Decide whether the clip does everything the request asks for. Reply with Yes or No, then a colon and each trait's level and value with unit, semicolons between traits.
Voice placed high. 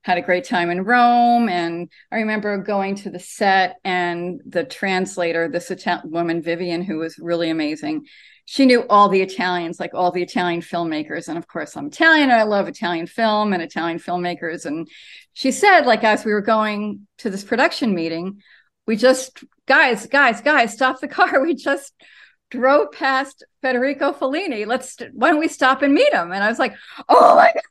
Yes: high, 210 Hz